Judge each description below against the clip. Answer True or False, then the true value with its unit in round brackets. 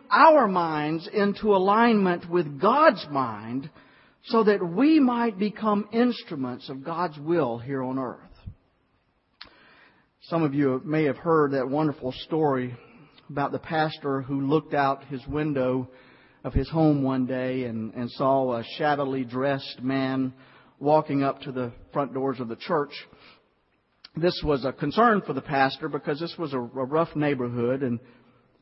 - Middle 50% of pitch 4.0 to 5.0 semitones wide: True (4.3 semitones)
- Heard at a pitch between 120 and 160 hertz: True (140 Hz)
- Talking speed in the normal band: True (150 wpm)